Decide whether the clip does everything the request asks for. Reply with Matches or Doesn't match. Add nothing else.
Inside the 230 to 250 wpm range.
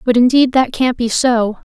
Doesn't match